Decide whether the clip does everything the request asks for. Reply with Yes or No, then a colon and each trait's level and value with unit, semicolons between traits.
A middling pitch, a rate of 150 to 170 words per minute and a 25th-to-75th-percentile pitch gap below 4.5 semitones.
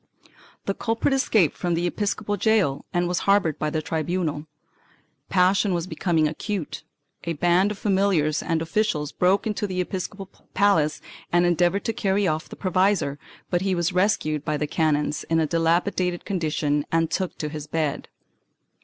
Yes: medium, 175 Hz; average, 160 wpm; average, 3.9 semitones